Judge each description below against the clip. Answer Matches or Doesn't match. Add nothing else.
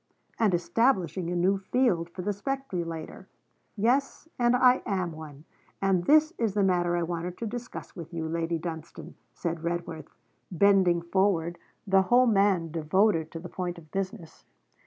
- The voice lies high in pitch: Doesn't match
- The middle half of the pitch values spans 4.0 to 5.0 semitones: Doesn't match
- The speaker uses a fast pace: Doesn't match